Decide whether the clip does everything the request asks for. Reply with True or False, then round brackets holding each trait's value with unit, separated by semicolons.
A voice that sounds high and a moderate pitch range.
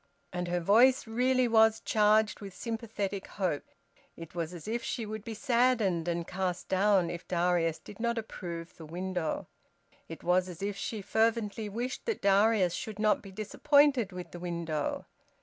True (200 Hz; 4.1 semitones)